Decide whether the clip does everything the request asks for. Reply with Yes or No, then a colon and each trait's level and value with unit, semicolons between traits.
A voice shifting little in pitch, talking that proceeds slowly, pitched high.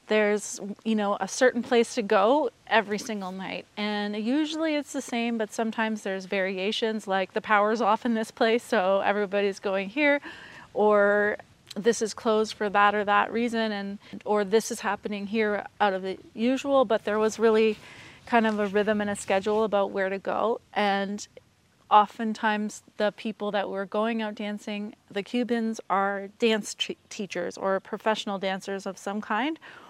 No: narrow, 2.0 semitones; average, 175 wpm; high, 210 Hz